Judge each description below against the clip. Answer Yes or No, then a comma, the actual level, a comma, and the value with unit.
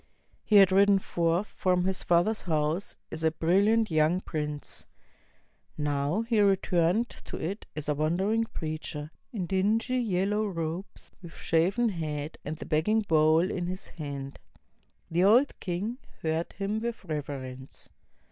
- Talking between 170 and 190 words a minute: No, average, 145 wpm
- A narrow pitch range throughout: No, average, 4.6 semitones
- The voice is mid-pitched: Yes, medium, 175 Hz